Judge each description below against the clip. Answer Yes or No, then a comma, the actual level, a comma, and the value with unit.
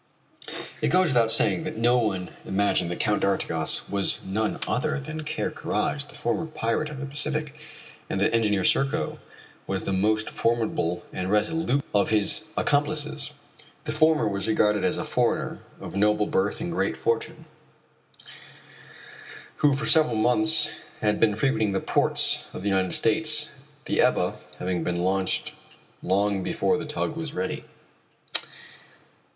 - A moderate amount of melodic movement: No, wide, 7.3 semitones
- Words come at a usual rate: Yes, average, 150 wpm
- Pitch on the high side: No, low, 115 Hz